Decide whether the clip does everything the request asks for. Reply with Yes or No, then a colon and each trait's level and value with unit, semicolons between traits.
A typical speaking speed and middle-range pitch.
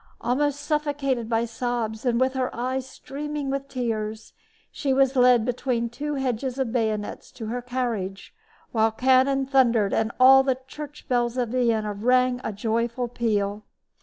No: average, 155 wpm; high, 245 Hz